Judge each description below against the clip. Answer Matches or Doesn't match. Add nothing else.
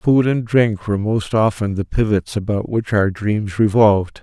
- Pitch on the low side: Matches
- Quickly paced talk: Doesn't match